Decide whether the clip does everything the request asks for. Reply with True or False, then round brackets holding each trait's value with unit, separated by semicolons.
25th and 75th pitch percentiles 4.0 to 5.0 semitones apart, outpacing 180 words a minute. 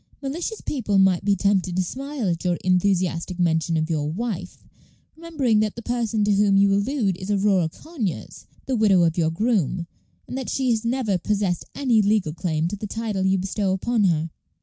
True (4.3 semitones; 190 wpm)